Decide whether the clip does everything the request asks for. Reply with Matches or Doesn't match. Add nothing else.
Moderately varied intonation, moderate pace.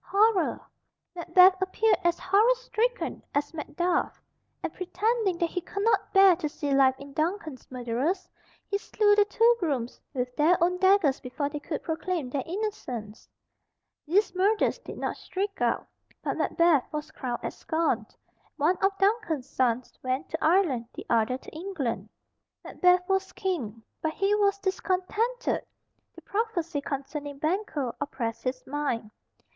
Doesn't match